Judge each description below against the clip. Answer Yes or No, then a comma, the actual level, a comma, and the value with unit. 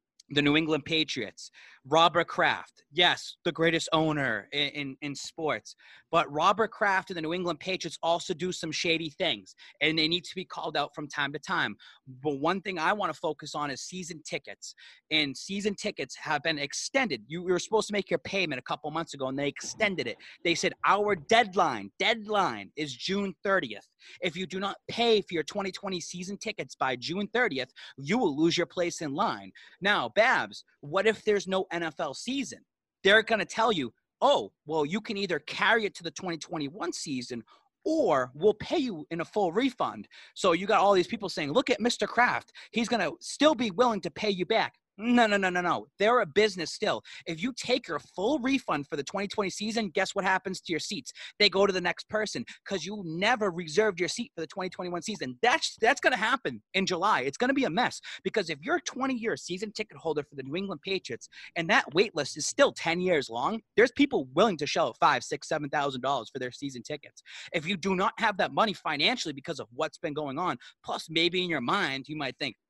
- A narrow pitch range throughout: No, average, 5.3 semitones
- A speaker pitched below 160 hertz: No, medium, 180 Hz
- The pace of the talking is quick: Yes, fast, 220 wpm